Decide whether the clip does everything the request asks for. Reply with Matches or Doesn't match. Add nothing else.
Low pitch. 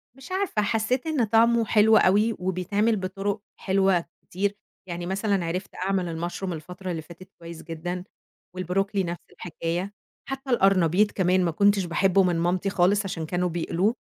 Doesn't match